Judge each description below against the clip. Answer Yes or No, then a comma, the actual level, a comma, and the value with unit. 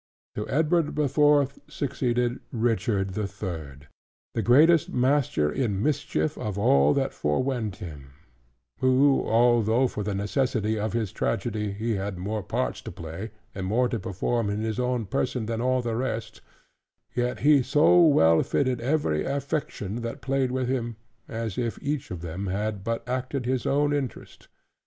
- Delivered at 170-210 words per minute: No, average, 160 wpm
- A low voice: Yes, low, 115 Hz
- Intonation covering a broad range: No, average, 4.5 semitones